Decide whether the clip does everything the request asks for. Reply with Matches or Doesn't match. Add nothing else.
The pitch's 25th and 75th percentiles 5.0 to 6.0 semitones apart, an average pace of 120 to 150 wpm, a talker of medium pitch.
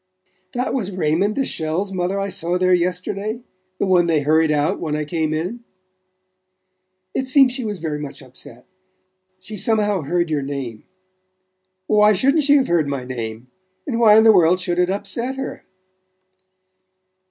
Doesn't match